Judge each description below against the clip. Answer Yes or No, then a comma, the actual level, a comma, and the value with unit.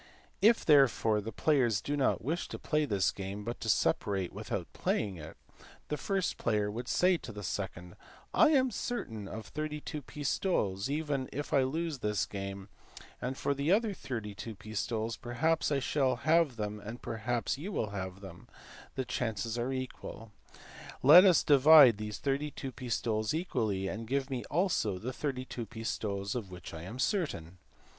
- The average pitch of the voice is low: Yes, low, 120 Hz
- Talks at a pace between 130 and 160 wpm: No, average, 170 wpm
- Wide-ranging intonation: Yes, wide, 5.8 semitones